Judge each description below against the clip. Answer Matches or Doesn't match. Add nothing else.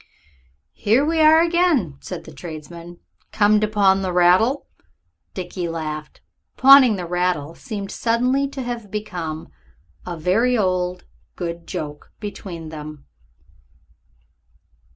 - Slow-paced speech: Matches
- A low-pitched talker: Doesn't match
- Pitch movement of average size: Doesn't match